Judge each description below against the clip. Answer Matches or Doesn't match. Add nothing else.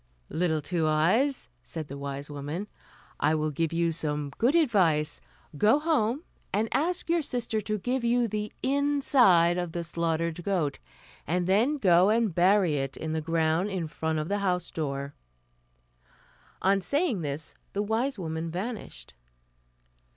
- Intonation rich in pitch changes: Matches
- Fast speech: Doesn't match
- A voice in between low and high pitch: Matches